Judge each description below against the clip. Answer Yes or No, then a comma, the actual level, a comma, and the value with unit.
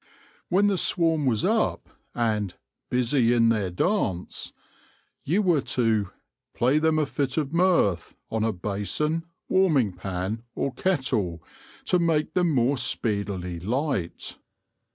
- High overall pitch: No, low, 125 Hz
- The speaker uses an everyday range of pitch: No, wide, 7.4 semitones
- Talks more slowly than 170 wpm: Yes, slow, 135 wpm